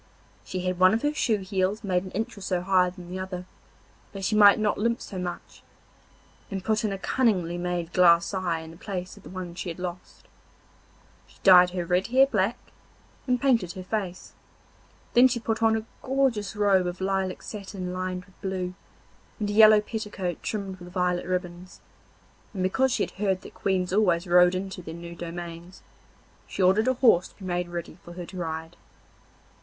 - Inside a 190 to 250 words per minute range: Yes, average, 195 wpm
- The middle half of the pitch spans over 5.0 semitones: No, average, 2.7 semitones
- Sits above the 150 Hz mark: Yes, medium, 185 Hz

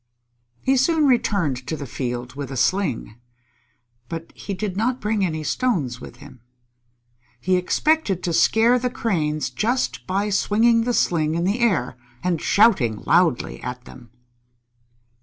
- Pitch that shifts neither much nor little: No, wide, 8.0 semitones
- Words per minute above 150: No, average, 145 wpm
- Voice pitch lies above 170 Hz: Yes, medium, 185 Hz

